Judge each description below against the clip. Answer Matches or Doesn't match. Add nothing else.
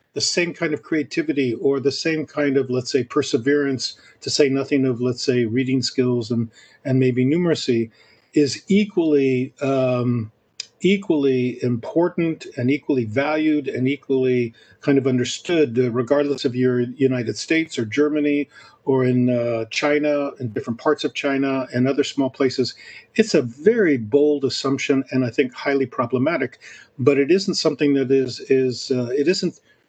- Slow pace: Doesn't match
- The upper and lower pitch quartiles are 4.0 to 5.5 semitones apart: Doesn't match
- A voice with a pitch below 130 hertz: Doesn't match